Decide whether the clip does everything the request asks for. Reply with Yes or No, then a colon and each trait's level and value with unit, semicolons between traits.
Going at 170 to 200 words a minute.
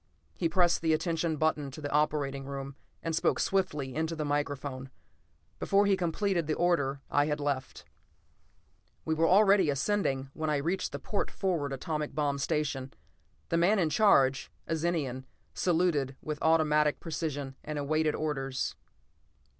No: average, 150 wpm